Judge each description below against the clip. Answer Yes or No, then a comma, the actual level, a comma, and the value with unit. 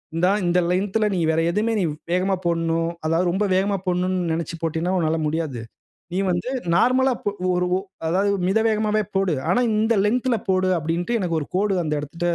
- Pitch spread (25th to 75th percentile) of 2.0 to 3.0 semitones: No, average, 3.6 semitones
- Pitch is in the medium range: Yes, medium, 180 Hz